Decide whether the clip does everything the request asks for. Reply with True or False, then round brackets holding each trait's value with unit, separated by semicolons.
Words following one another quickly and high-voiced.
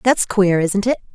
True (210 wpm; 200 Hz)